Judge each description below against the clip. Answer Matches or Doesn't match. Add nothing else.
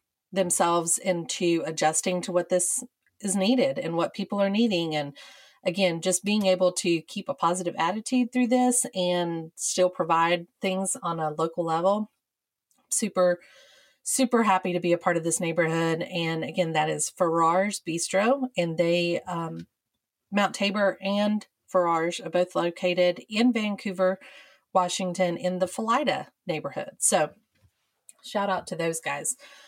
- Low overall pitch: Doesn't match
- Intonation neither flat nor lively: Matches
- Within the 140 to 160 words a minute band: Matches